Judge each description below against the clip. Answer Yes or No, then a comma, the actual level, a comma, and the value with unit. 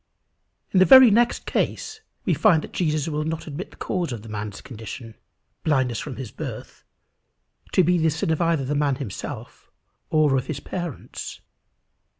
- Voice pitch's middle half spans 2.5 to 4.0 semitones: No, average, 4.8 semitones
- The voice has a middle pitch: Yes, medium, 150 Hz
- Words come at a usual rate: Yes, average, 170 wpm